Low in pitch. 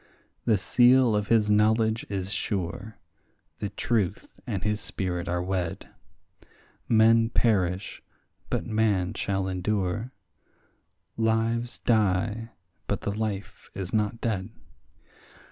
Yes: low, 105 Hz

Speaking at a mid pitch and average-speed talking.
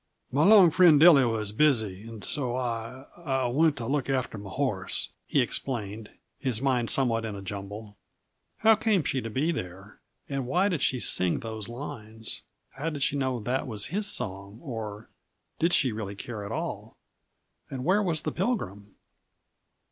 No: low, 125 Hz; average, 170 wpm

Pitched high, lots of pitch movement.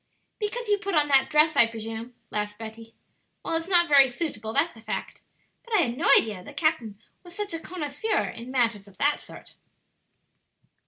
Yes: very high, 280 Hz; wide, 6.8 semitones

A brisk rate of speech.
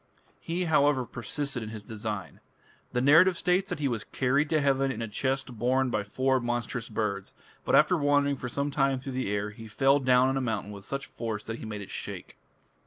Yes: fast, 220 wpm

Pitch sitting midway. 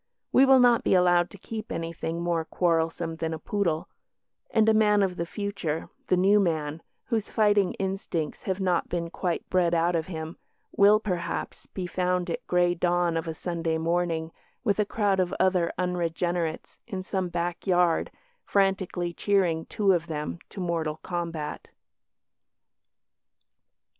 Yes: medium, 175 Hz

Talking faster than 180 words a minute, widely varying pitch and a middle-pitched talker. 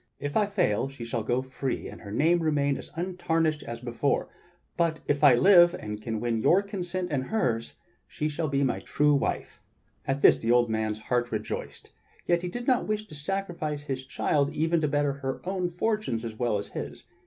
Yes: average, 200 wpm; wide, 6.2 semitones; medium, 145 Hz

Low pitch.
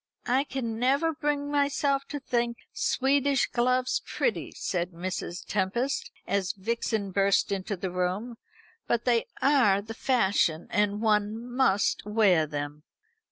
No: high, 225 Hz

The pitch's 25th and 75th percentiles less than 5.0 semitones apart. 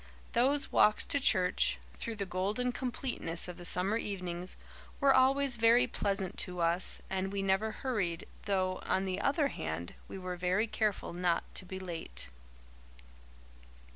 Yes: average, 4.2 semitones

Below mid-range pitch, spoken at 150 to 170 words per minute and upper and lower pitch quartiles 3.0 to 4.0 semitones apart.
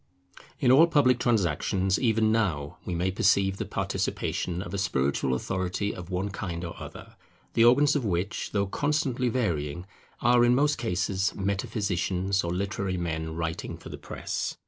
No: very low, 95 Hz; average, 160 wpm; average, 4.8 semitones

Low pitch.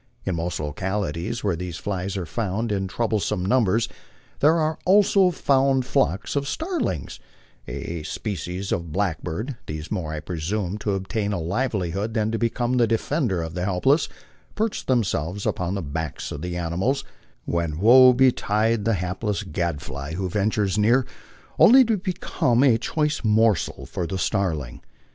Yes: low, 100 Hz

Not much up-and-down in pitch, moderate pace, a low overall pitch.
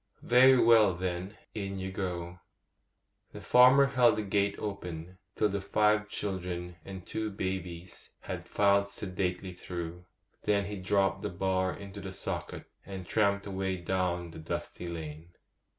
Yes: narrow, 2.3 semitones; average, 145 wpm; very low, 95 Hz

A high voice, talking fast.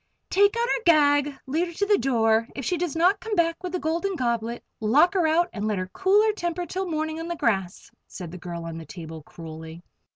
Yes: very high, 310 Hz; fast, 235 wpm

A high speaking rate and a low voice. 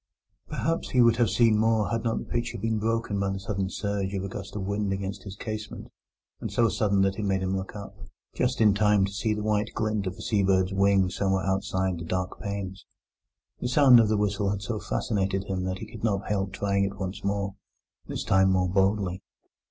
Yes: fast, 215 wpm; low, 100 Hz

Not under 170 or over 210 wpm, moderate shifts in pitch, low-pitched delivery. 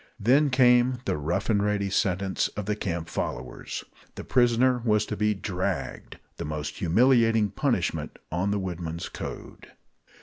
No: average, 145 wpm; average, 4.5 semitones; low, 105 Hz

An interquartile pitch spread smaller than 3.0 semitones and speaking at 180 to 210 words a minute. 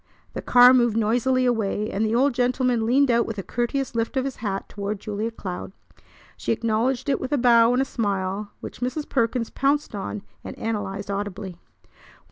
No: average, 3.4 semitones; average, 185 wpm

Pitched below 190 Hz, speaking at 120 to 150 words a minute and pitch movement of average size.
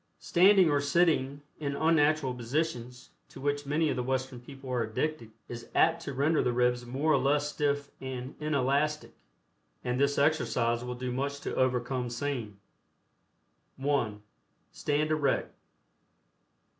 Yes: medium, 140 Hz; average, 140 wpm; average, 3.1 semitones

